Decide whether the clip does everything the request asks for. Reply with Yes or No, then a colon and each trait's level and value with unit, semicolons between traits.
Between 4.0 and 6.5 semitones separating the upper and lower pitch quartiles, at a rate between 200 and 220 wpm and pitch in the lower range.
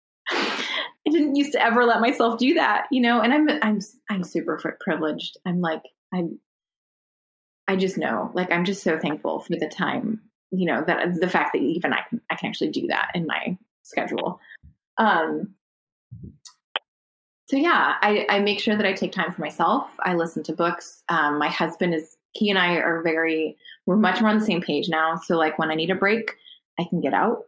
No: average, 4.9 semitones; fast, 205 wpm; medium, 185 Hz